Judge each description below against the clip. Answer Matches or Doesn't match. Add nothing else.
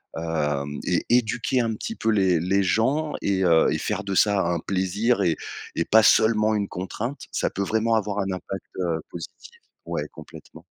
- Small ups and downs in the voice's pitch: Doesn't match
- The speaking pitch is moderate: Doesn't match